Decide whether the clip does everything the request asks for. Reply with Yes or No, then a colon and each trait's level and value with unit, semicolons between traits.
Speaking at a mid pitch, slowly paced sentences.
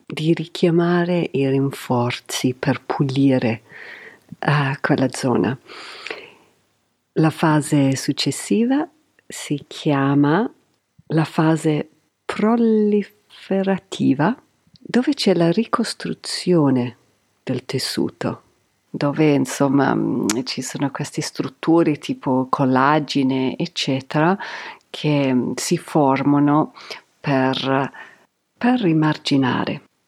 Yes: medium, 150 Hz; slow, 80 wpm